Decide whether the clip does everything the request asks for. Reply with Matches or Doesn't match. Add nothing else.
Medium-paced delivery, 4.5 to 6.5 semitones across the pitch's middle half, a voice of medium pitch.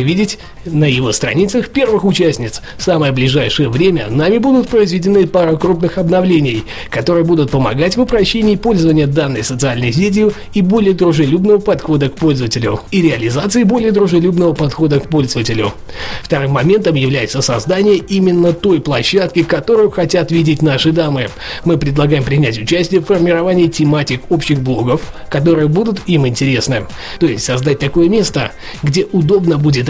Matches